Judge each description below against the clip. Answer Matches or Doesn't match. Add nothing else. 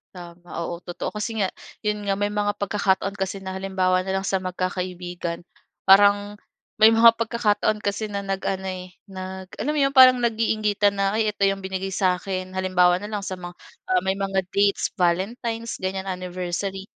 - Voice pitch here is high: Matches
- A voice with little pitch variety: Matches